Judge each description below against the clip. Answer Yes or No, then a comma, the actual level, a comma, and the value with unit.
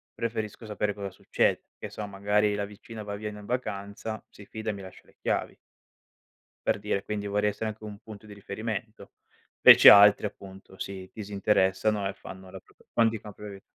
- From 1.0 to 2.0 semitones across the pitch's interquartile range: Yes, narrow, 1.4 semitones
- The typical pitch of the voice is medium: No, low, 105 Hz